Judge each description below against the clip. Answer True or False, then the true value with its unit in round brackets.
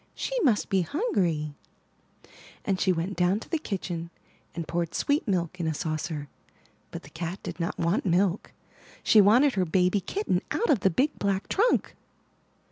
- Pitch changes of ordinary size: True (4.2 semitones)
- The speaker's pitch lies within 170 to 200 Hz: True (185 Hz)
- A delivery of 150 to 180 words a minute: True (170 wpm)